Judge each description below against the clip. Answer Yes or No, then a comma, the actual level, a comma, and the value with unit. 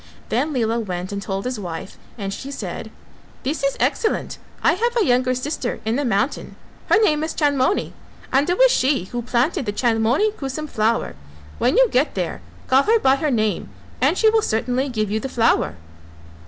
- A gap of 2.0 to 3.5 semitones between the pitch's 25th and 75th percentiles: No, average, 5.3 semitones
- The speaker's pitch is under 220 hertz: No, very high, 255 Hz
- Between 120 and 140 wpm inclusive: No, average, 190 wpm